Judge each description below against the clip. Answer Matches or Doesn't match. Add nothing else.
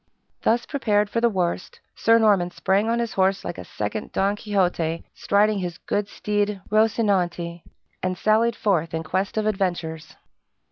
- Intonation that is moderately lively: Matches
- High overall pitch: Matches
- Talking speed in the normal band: Matches